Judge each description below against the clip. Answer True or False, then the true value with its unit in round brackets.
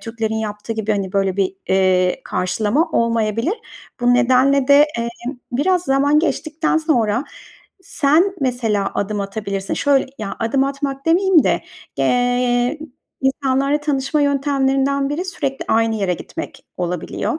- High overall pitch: True (260 Hz)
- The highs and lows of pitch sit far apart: False (4.8 semitones)